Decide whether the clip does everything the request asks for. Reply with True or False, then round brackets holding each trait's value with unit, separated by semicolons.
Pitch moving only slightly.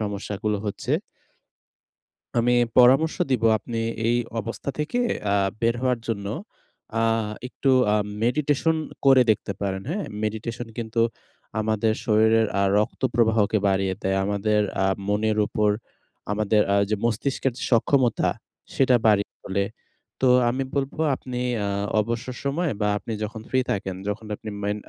False (3.3 semitones)